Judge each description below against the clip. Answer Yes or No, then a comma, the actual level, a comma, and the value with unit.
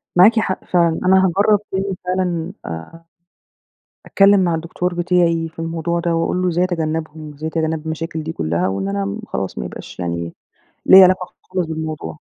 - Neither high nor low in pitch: Yes, medium, 165 Hz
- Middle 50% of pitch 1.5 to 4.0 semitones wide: Yes, narrow, 2.6 semitones